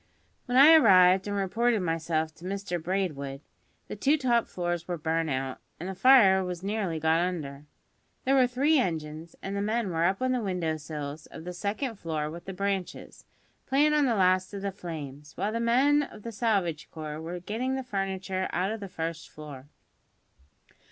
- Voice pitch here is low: No, medium, 185 Hz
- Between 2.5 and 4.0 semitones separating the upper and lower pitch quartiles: No, wide, 5.4 semitones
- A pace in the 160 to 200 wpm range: Yes, average, 190 wpm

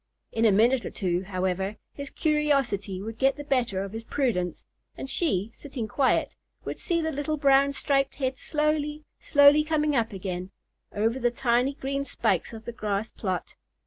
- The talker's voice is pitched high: Yes, very high, 255 Hz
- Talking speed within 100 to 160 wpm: No, average, 175 wpm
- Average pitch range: No, wide, 5.8 semitones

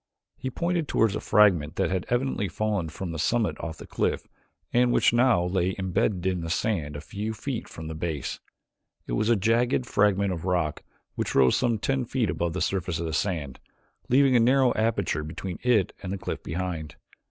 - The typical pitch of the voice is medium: No, very low, 95 Hz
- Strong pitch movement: Yes, wide, 5.7 semitones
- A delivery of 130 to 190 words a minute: No, average, 200 wpm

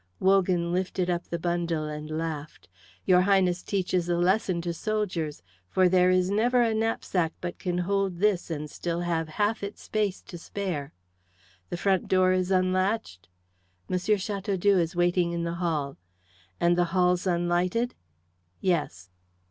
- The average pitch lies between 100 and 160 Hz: No, medium, 180 Hz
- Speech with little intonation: Yes, narrow, 2.1 semitones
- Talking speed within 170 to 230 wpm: No, average, 150 wpm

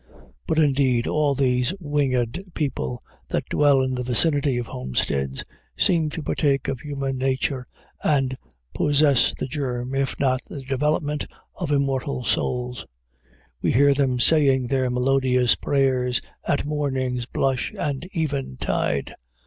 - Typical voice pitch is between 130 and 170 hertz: Yes, low, 135 Hz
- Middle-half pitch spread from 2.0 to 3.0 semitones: Yes, narrow, 2.4 semitones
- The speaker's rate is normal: No, slow, 130 wpm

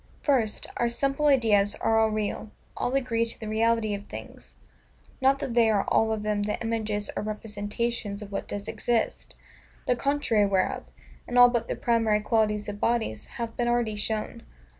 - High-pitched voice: Yes, high, 225 Hz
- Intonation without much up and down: Yes, narrow, 2.3 semitones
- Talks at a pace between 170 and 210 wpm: Yes, average, 180 wpm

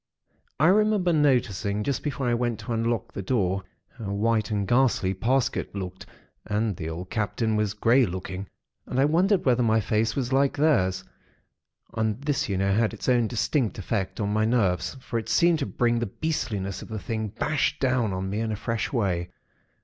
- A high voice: No, low, 110 Hz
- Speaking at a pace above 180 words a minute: Yes, average, 190 wpm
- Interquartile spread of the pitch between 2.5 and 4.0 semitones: No, average, 4.4 semitones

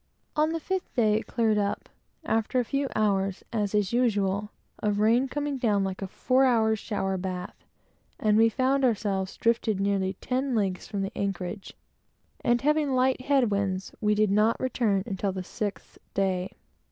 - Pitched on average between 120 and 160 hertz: No, high, 215 Hz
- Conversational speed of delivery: Yes, average, 170 wpm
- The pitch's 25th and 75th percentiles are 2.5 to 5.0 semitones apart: Yes, average, 4.2 semitones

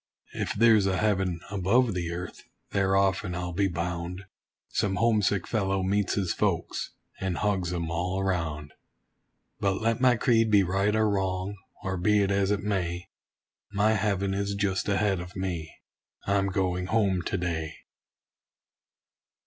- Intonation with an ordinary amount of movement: No, narrow, 2.3 semitones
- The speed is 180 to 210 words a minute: No, average, 150 wpm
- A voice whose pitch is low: Yes, very low, 95 Hz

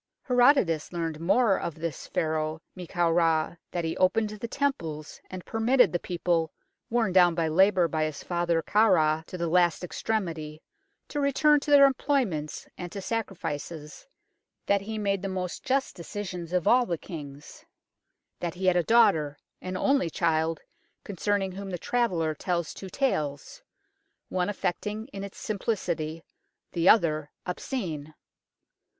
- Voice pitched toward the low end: No, medium, 180 Hz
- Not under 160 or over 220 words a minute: No, average, 150 wpm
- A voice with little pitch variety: No, average, 4.5 semitones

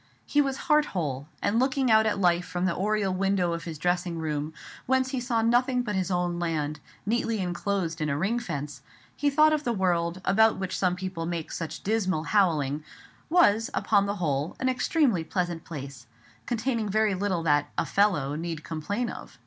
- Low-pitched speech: No, medium, 185 Hz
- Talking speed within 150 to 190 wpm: Yes, average, 185 wpm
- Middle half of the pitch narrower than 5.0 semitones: No, average, 5.3 semitones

